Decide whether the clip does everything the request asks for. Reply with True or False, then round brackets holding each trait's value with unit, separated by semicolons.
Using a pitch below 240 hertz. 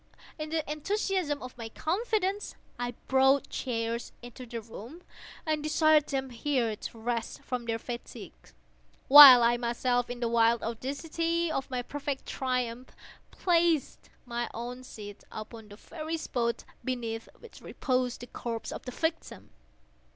False (255 Hz)